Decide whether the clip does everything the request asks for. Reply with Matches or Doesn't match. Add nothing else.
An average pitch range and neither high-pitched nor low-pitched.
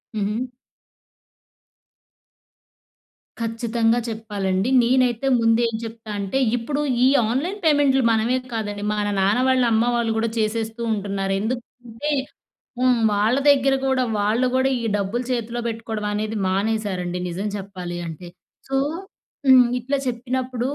Doesn't match